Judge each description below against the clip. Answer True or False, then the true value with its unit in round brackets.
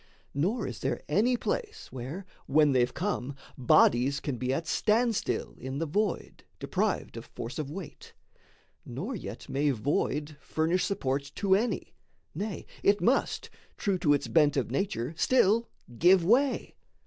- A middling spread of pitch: False (6.8 semitones)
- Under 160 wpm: True (150 wpm)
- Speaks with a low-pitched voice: False (160 Hz)